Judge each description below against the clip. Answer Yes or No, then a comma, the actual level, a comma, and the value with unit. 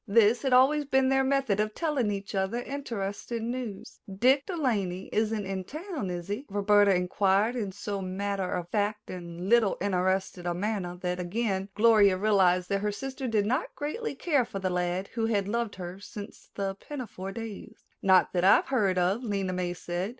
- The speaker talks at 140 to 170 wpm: No, average, 185 wpm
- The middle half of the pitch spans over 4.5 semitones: No, average, 3.9 semitones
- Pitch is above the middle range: Yes, high, 205 Hz